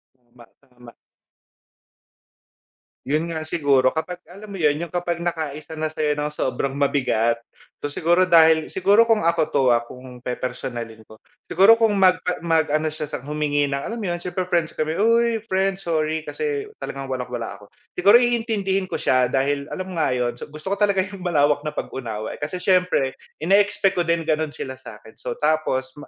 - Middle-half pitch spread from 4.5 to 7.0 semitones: Yes, average, 5.3 semitones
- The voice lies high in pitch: No, medium, 155 Hz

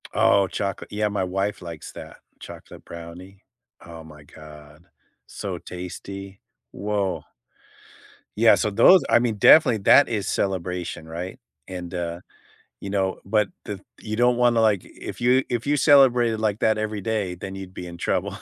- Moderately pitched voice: No, low, 100 Hz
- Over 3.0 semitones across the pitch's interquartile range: Yes, average, 3.6 semitones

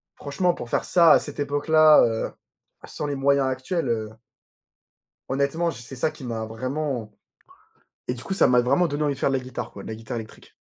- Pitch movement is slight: No, average, 4.1 semitones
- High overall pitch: No, low, 135 Hz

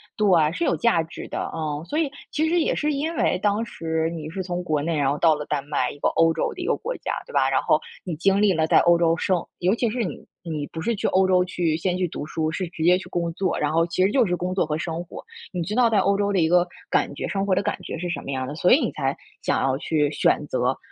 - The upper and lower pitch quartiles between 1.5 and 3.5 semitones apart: No, average, 3.9 semitones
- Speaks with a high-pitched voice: No, medium, 175 Hz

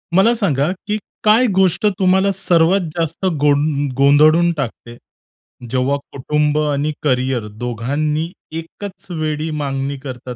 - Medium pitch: Yes, medium, 150 Hz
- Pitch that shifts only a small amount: No, average, 4.0 semitones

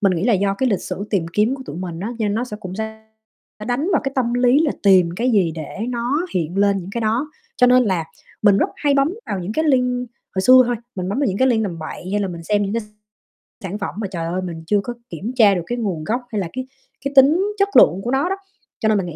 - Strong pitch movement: No, average, 5.0 semitones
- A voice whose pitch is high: Yes, high, 210 Hz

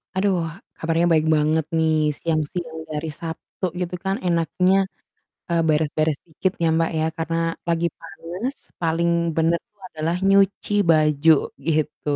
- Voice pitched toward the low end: No, medium, 165 Hz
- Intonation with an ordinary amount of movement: No, narrow, 1.7 semitones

